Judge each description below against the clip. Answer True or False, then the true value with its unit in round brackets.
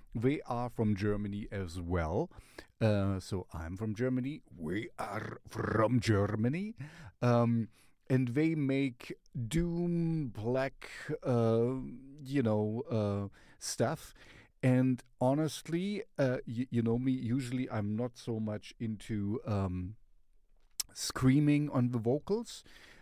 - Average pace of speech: False (115 wpm)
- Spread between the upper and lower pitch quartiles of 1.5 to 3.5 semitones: False (4.0 semitones)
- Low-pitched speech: True (125 Hz)